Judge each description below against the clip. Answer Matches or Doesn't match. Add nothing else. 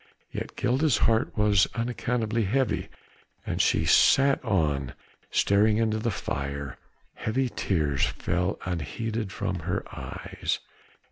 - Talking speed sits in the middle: Doesn't match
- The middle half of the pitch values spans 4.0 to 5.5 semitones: Matches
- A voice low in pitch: Matches